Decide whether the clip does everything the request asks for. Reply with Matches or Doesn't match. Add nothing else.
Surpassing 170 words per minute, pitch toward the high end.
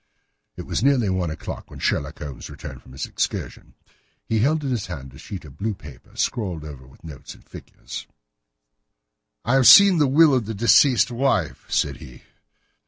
Doesn't match